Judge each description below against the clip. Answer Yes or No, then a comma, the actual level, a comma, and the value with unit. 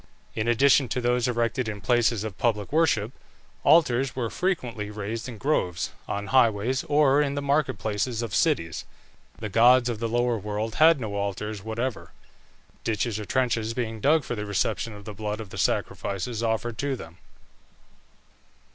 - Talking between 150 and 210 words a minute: Yes, average, 165 wpm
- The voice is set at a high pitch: No, low, 115 Hz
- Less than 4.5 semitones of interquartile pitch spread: Yes, average, 3.3 semitones